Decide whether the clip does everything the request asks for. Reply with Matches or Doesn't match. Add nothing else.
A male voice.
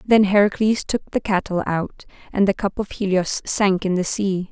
Doesn't match